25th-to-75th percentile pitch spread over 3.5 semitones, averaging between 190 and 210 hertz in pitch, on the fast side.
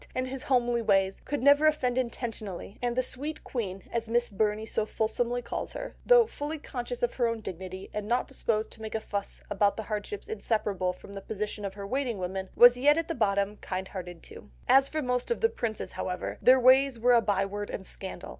No: average, 4.2 semitones; high, 230 Hz; fast, 215 wpm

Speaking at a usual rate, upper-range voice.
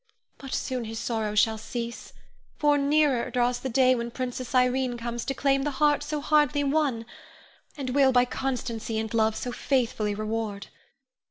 Yes: average, 170 wpm; very high, 250 Hz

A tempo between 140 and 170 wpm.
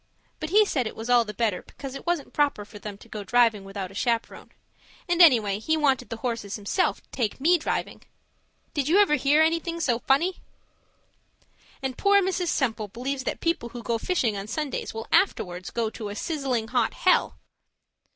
No: average, 190 wpm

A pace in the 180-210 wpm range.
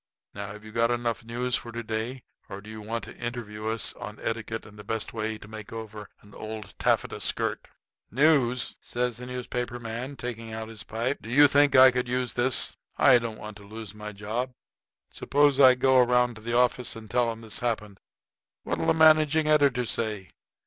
Yes: average, 200 wpm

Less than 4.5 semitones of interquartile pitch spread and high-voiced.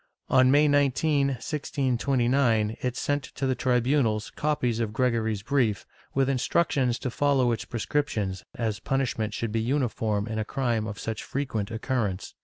No: average, 3.7 semitones; low, 125 Hz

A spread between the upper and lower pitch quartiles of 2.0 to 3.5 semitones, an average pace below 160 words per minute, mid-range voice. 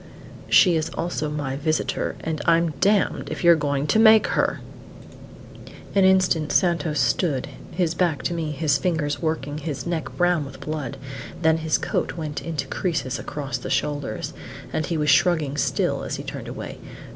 No: average, 2.8 semitones; average, 170 wpm; medium, 155 Hz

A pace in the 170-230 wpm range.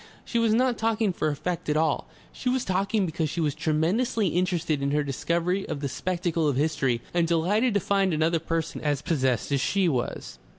Yes: average, 200 wpm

